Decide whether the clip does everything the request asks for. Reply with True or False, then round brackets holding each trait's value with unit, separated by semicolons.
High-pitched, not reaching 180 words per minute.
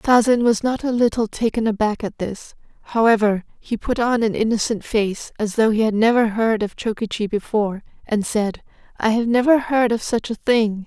False (220 Hz; 190 wpm)